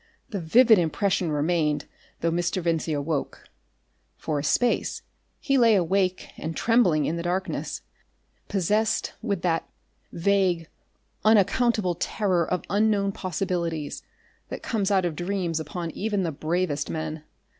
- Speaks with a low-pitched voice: No, medium, 180 Hz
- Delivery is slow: Yes, slow, 130 wpm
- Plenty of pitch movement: No, average, 3.6 semitones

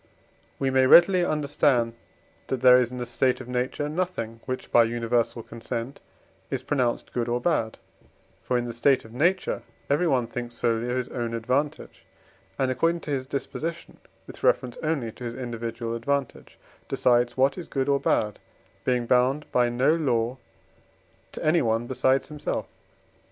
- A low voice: Yes, low, 125 Hz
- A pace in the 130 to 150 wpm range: No, average, 160 wpm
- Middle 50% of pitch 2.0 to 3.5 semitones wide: Yes, average, 3.0 semitones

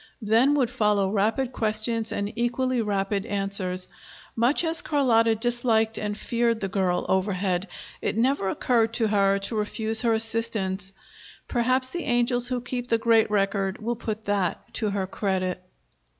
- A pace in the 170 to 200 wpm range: No, average, 150 wpm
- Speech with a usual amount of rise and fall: Yes, average, 3.3 semitones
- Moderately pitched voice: No, high, 220 Hz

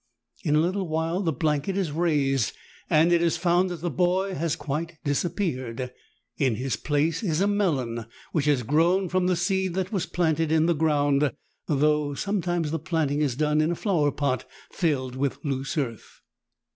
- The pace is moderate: Yes, average, 185 wpm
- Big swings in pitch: No, average, 3.5 semitones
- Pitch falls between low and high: Yes, medium, 160 Hz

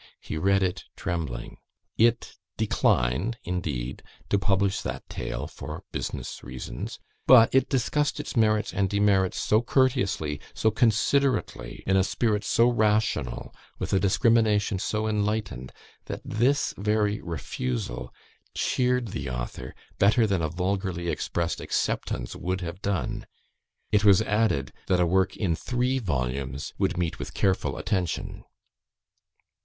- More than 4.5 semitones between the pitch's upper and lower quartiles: Yes, average, 5.1 semitones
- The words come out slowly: Yes, slow, 130 wpm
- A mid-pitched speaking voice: No, low, 100 Hz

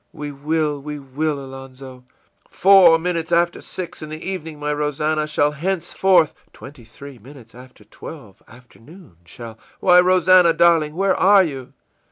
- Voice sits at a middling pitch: Yes, medium, 150 Hz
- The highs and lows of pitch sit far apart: No, average, 4.3 semitones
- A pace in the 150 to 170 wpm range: Yes, average, 160 wpm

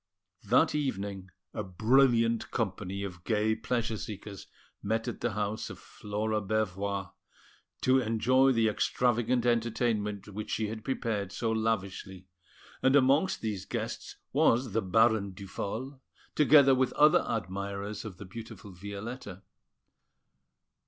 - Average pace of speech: No, slow, 125 wpm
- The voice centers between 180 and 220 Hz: No, low, 110 Hz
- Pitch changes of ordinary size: Yes, average, 3.2 semitones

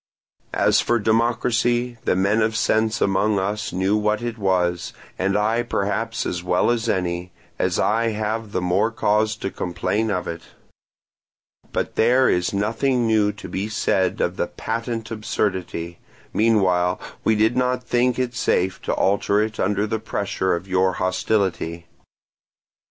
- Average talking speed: Yes, average, 150 wpm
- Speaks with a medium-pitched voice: No, low, 105 Hz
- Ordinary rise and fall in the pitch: Yes, average, 3.3 semitones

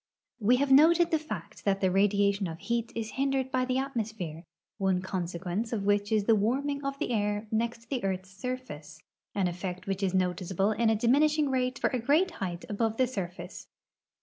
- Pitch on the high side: Yes, high, 215 Hz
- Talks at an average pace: Yes, average, 190 wpm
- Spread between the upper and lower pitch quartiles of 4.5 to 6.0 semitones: Yes, average, 5.0 semitones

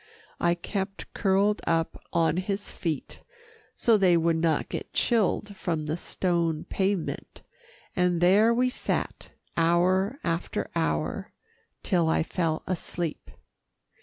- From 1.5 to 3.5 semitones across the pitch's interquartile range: Yes, average, 3.0 semitones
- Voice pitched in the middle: Yes, medium, 175 Hz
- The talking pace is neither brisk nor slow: No, slow, 120 wpm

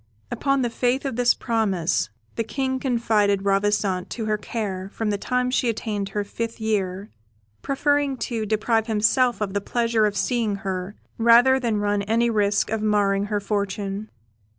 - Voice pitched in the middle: No, high, 215 Hz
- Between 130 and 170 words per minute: Yes, average, 165 wpm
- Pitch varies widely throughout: No, average, 2.8 semitones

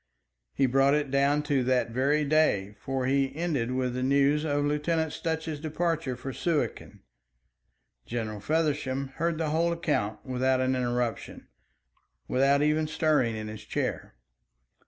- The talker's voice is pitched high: No, medium, 140 Hz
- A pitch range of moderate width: Yes, average, 3.3 semitones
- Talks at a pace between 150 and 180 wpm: No, average, 140 wpm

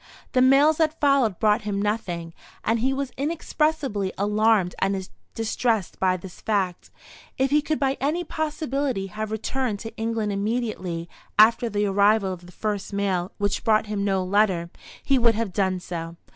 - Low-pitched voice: No, high, 215 Hz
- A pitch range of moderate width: Yes, average, 5.0 semitones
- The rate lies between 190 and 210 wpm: No, average, 165 wpm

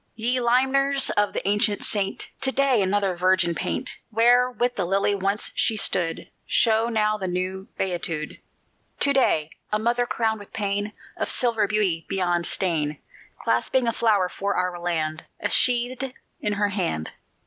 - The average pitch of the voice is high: Yes, high, 205 Hz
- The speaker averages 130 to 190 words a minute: Yes, average, 160 wpm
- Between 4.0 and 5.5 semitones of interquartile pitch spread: Yes, average, 4.5 semitones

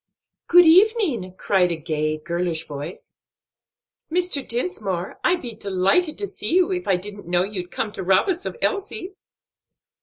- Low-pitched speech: No, high, 205 Hz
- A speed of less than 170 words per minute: Yes, average, 155 wpm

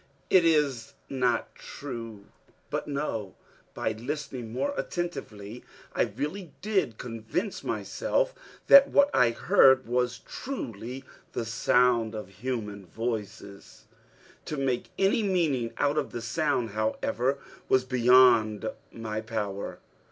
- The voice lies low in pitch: Yes, low, 125 Hz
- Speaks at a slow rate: Yes, slow, 115 wpm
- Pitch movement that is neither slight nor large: Yes, average, 4.8 semitones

